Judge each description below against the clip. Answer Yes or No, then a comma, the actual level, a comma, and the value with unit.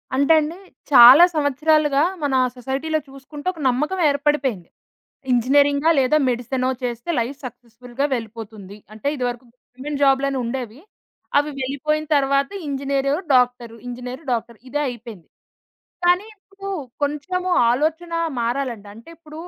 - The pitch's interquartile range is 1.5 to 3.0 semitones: No, average, 3.4 semitones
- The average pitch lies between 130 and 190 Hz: No, very high, 270 Hz